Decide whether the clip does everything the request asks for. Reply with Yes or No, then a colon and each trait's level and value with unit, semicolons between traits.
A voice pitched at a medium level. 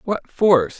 Yes: medium, 170 Hz